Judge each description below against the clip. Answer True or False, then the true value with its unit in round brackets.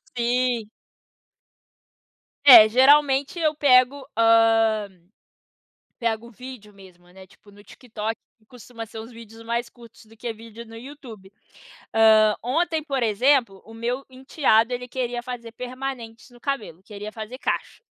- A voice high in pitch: True (235 Hz)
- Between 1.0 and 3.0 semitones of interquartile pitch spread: True (2.6 semitones)